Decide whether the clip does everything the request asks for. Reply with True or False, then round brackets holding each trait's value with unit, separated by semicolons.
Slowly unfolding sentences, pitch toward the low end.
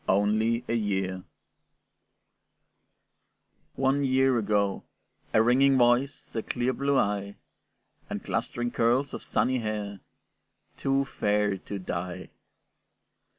True (105 wpm; 115 Hz)